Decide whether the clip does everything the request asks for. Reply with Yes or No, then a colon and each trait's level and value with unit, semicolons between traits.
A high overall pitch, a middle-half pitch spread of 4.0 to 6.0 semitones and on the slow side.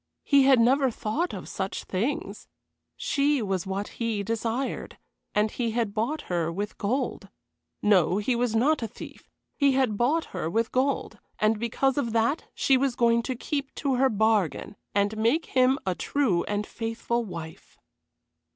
No: high, 230 Hz; average, 4.4 semitones; average, 165 wpm